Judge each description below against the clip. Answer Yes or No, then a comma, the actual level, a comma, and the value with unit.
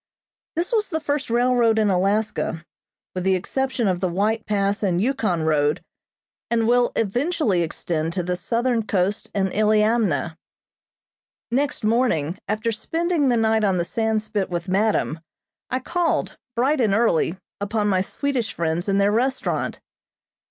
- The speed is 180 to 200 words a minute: No, average, 145 wpm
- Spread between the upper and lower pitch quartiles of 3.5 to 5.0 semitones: Yes, average, 4.7 semitones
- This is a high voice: Yes, high, 215 Hz